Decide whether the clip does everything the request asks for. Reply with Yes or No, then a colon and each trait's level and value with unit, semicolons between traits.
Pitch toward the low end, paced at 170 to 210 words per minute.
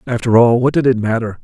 No: low, 120 Hz; fast, 250 wpm